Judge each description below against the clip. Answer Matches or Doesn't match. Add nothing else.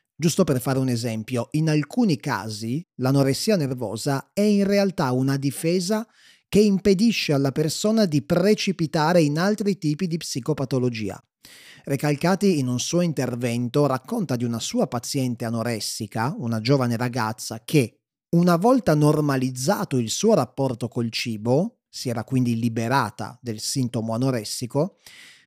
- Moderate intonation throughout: Doesn't match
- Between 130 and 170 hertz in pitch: Matches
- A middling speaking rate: Matches